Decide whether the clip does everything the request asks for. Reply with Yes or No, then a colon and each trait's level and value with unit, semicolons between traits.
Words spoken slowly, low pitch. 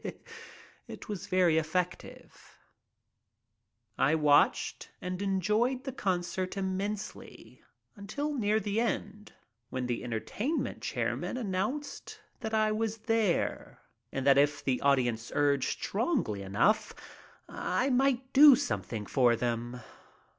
No: slow, 125 wpm; high, 190 Hz